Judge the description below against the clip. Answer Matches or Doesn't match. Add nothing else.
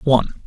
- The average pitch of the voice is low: Matches